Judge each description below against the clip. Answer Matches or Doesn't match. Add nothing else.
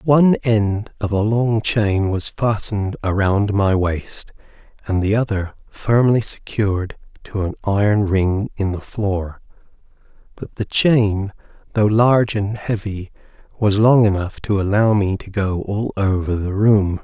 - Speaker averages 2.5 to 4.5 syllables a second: Matches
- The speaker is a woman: Doesn't match